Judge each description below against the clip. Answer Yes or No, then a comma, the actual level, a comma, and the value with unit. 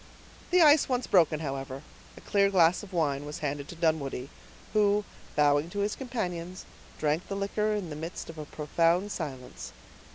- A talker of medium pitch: Yes, medium, 170 Hz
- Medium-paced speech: Yes, average, 170 wpm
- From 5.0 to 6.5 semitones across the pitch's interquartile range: Yes, average, 5.3 semitones